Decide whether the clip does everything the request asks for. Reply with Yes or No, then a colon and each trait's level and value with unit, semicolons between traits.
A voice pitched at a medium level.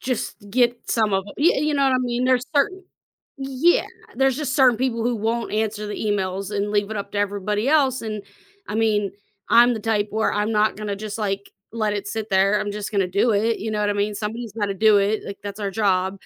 No: high, 215 Hz